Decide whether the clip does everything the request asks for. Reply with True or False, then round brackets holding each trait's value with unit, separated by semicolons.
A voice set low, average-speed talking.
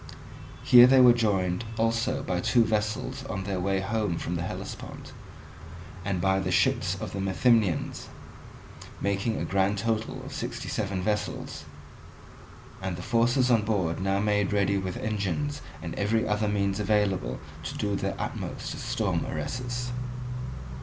True (105 Hz; 150 wpm)